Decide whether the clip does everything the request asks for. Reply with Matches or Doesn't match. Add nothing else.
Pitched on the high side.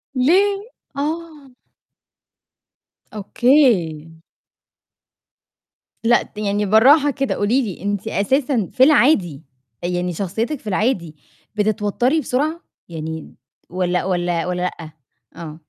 Matches